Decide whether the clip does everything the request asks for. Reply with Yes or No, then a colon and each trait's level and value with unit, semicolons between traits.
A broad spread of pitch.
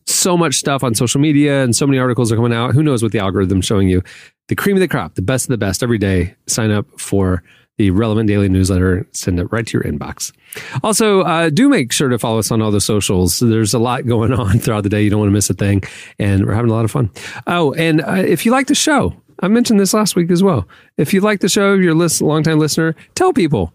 Yes: wide, 8.1 semitones